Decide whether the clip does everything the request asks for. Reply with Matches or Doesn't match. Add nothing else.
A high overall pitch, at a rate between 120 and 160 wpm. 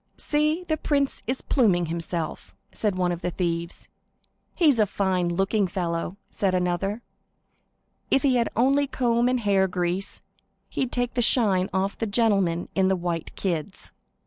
Matches